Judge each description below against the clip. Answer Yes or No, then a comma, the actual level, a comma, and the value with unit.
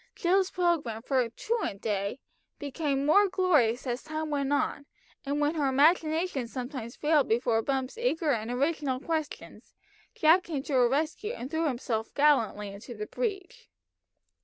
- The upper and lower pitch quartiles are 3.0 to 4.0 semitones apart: No, average, 4.8 semitones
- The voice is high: Yes, very high, 285 Hz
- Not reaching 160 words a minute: Yes, average, 150 wpm